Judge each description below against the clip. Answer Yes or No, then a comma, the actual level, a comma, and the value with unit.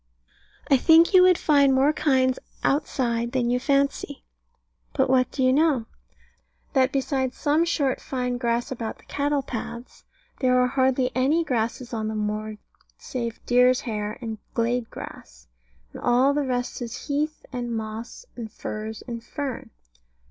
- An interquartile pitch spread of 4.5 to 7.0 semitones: No, average, 3.0 semitones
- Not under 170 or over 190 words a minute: No, average, 155 wpm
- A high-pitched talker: Yes, very high, 255 Hz